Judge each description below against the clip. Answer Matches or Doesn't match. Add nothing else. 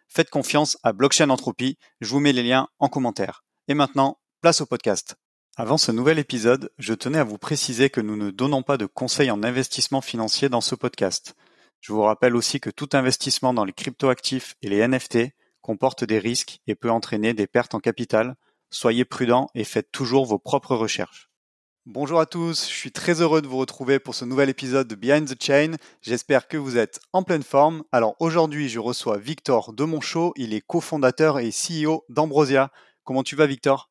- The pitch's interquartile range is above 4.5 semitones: Doesn't match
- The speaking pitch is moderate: Doesn't match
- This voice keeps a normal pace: Matches